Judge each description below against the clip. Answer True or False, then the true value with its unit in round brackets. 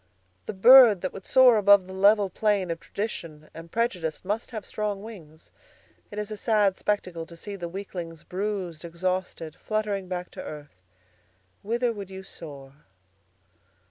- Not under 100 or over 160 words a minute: True (155 wpm)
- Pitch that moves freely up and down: False (3.8 semitones)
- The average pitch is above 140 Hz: True (190 Hz)